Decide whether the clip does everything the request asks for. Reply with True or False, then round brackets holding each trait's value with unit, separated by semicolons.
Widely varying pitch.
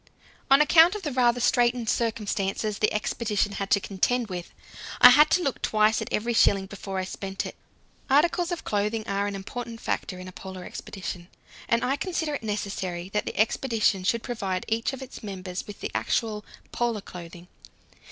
False (4.0 semitones)